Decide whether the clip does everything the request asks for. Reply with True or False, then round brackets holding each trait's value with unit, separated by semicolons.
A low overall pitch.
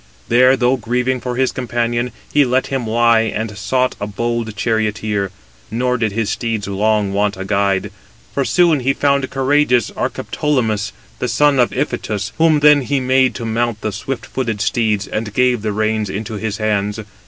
True (115 Hz)